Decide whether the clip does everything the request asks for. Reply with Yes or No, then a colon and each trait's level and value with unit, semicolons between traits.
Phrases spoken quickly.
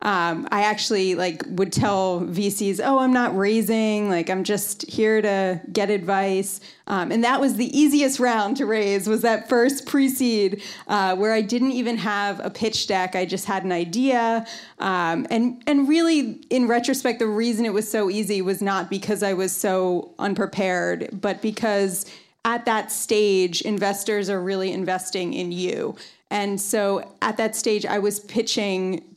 No: average, 170 wpm